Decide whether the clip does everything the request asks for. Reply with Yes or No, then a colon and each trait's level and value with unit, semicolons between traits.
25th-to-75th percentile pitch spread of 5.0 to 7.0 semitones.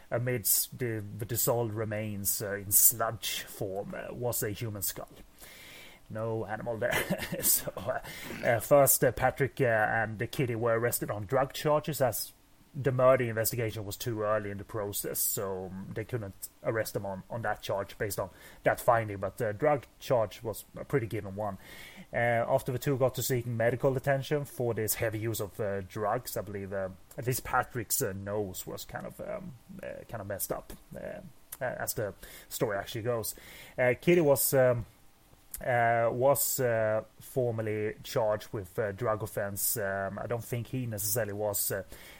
No: average, 3.6 semitones